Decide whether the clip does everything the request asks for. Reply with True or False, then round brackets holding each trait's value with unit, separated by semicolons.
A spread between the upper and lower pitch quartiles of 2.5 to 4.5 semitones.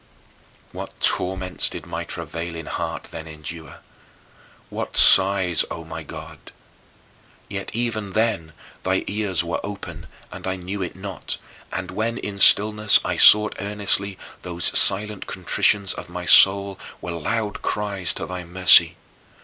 True (3.0 semitones)